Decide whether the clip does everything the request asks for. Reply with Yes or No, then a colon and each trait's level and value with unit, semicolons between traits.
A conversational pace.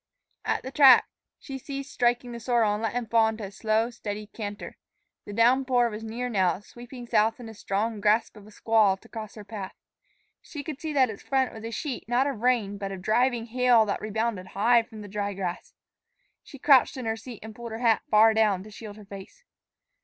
No: fast, 220 wpm